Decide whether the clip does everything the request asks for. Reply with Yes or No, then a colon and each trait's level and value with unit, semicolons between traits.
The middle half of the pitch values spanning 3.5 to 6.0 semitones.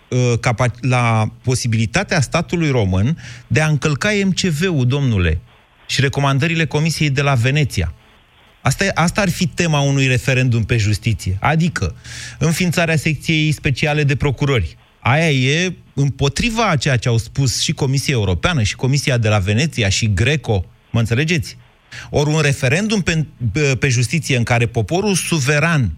Yes: average, 4.9 semitones